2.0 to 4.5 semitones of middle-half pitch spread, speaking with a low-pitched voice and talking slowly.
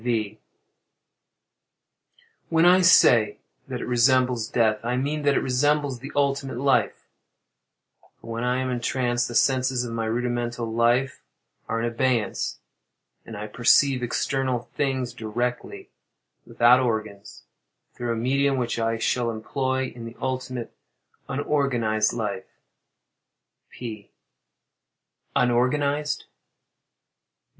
Yes: narrow, 2.4 semitones; low, 125 Hz; slow, 115 wpm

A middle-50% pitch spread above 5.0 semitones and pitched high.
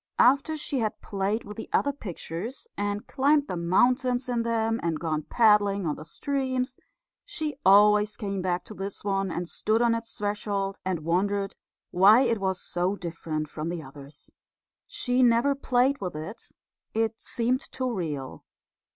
Yes: wide, 5.4 semitones; high, 205 Hz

